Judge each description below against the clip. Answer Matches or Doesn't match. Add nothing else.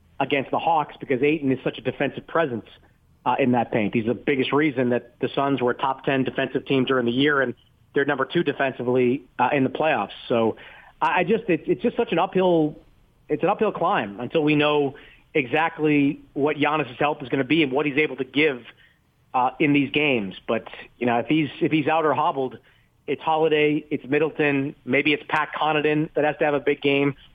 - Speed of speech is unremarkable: Doesn't match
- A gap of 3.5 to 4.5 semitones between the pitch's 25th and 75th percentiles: Doesn't match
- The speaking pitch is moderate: Matches